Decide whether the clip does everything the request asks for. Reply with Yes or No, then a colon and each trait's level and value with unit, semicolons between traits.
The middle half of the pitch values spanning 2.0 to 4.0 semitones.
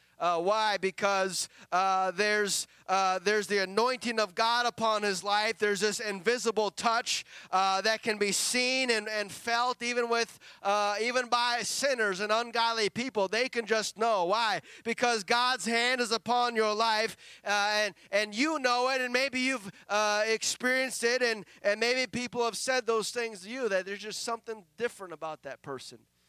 Yes: average, 2.9 semitones